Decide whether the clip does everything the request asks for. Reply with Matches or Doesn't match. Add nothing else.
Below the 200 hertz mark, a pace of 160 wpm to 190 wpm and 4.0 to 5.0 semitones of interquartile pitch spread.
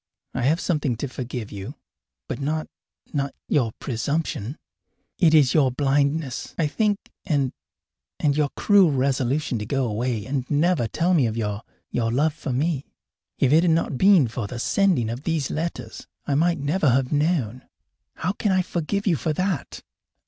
Matches